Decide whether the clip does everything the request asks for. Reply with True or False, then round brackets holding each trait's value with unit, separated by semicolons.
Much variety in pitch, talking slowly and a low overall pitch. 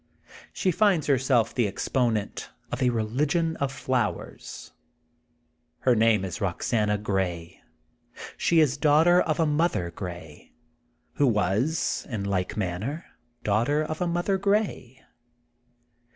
True (7.0 semitones; 120 wpm; 125 Hz)